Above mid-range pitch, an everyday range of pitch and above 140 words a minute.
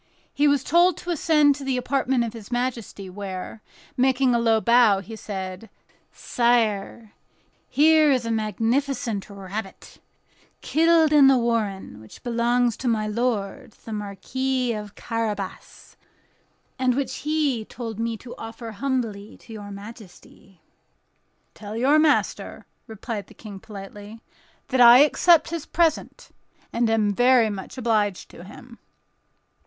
No: high, 230 Hz; average, 4.0 semitones; slow, 135 wpm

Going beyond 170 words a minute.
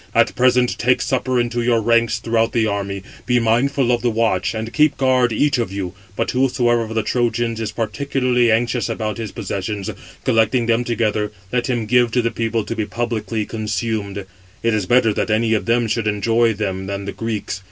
Yes: average, 200 wpm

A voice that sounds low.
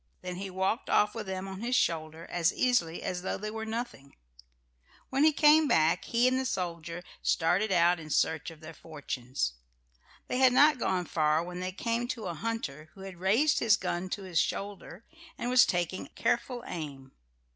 No: medium, 185 Hz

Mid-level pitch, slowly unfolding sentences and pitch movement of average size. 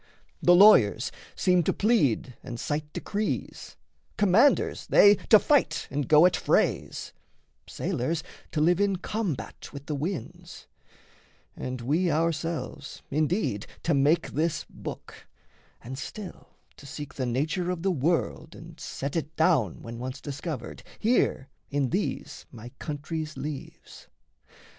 Yes: medium, 155 Hz; slow, 130 wpm; average, 4.5 semitones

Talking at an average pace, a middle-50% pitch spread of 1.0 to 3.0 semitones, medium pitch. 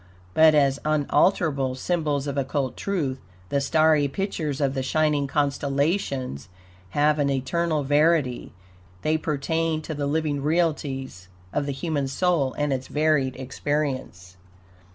No: slow, 130 wpm; narrow, 2.6 semitones; medium, 145 Hz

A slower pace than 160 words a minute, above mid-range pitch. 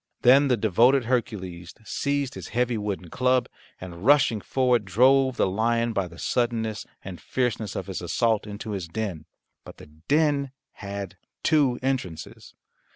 No: average, 150 wpm; low, 115 Hz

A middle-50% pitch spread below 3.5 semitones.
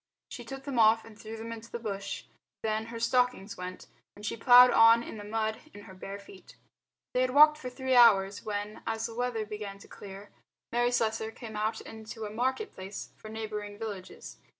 Yes: narrow, 2.4 semitones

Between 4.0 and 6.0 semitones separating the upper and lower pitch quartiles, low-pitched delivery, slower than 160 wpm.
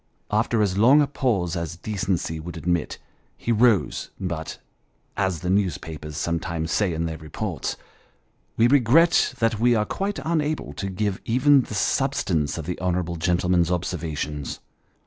Yes: wide, 5.6 semitones; very low, 90 Hz; average, 150 wpm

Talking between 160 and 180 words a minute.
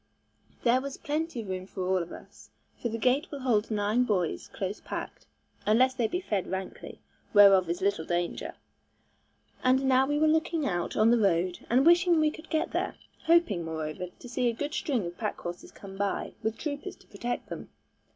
No: average, 195 wpm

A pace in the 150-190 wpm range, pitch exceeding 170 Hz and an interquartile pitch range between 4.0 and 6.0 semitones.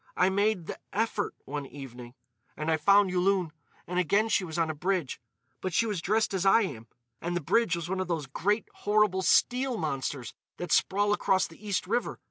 No: average, 200 wpm; medium, 185 Hz; average, 4.4 semitones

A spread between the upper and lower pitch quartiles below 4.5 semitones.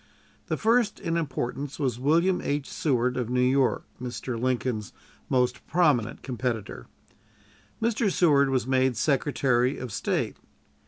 Yes: average, 3.4 semitones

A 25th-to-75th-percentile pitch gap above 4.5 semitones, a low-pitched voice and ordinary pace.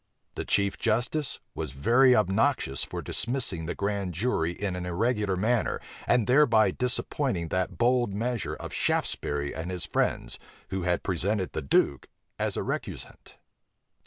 Yes: wide, 5.6 semitones; low, 100 Hz; average, 145 wpm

